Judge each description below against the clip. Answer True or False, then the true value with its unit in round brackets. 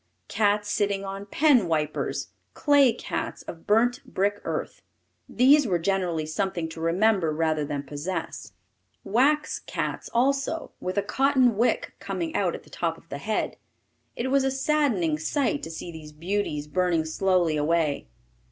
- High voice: True (195 Hz)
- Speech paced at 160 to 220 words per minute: False (150 wpm)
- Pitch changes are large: True (7.4 semitones)